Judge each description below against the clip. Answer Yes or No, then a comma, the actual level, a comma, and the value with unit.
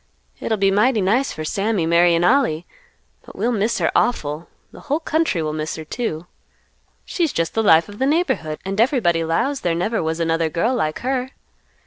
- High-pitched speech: Yes, high, 195 Hz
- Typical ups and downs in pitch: No, wide, 7.1 semitones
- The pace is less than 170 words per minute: No, average, 185 wpm